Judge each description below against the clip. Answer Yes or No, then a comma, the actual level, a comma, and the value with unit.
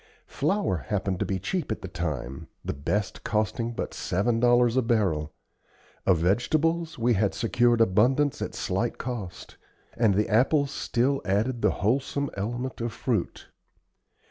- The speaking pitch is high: No, low, 115 Hz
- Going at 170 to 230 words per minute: No, average, 145 wpm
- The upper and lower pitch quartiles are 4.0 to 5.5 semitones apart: Yes, average, 4.4 semitones